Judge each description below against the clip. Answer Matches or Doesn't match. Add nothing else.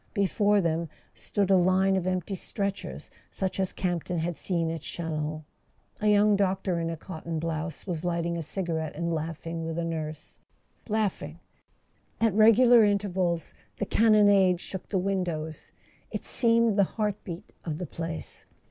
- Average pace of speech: Matches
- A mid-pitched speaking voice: Matches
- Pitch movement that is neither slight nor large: Matches